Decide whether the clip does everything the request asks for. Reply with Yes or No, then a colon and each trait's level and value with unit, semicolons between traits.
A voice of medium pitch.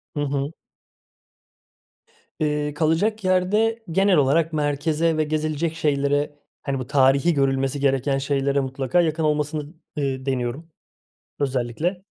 Yes: medium, 150 Hz